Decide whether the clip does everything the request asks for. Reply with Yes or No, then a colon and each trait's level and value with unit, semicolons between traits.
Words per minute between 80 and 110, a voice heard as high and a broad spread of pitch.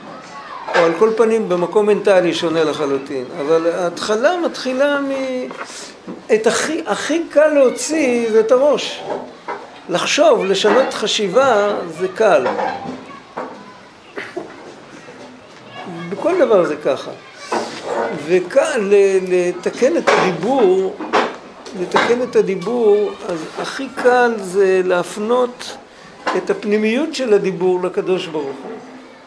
Yes: slow, 100 wpm; high, 215 Hz; wide, 6.1 semitones